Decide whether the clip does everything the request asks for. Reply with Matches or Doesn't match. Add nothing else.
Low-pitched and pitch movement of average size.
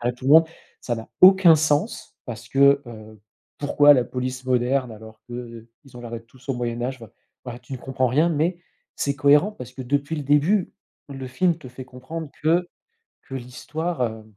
Matches